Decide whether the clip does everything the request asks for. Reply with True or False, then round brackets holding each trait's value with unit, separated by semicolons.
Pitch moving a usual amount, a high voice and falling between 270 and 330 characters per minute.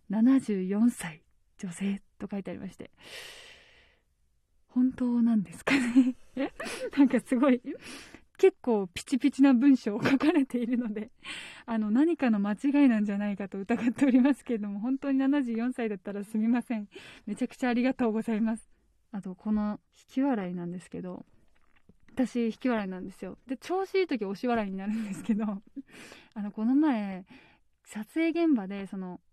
True (4.4 semitones; 235 Hz; 315 characters per minute)